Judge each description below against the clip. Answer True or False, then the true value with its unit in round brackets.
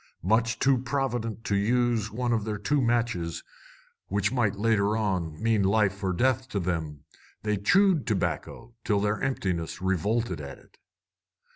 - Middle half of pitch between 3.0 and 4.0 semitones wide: True (3.7 semitones)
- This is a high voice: False (110 Hz)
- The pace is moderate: True (150 wpm)